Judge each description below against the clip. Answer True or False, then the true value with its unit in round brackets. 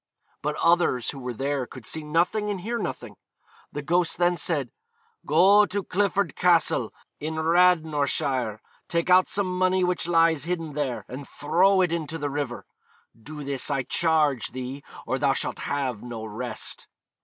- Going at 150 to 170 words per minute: True (160 wpm)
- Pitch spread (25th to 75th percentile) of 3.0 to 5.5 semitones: True (4.6 semitones)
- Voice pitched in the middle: True (155 Hz)